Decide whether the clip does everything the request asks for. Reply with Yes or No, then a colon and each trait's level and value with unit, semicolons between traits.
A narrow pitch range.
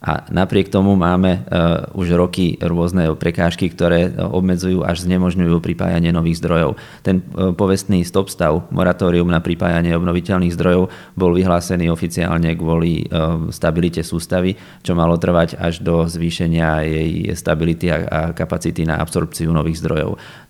Yes: narrow, 1.4 semitones